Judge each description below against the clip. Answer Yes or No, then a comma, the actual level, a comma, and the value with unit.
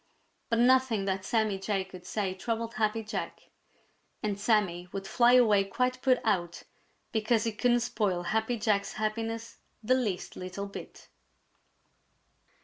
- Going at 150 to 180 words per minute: No, average, 140 wpm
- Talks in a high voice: Yes, high, 215 Hz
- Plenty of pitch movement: No, average, 3.0 semitones